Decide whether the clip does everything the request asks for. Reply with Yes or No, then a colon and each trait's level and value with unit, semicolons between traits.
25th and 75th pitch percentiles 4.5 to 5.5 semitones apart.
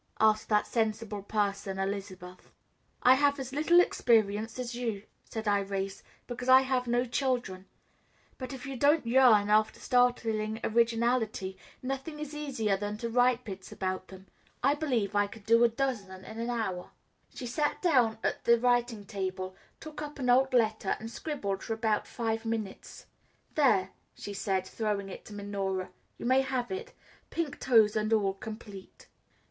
No: average, 3.9 semitones